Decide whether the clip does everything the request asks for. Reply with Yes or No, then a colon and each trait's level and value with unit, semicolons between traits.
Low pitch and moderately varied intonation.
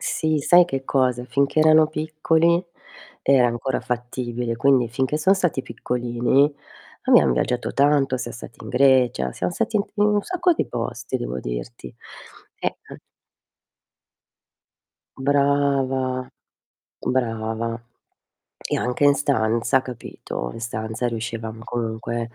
Yes: low, 130 Hz; average, 3.6 semitones